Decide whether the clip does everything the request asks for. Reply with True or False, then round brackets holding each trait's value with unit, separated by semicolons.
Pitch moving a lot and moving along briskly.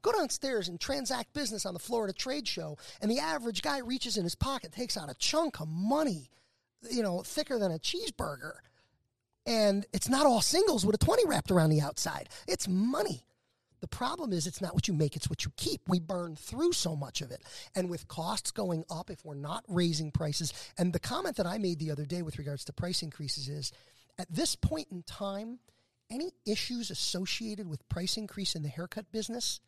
True (6.8 semitones; 210 wpm)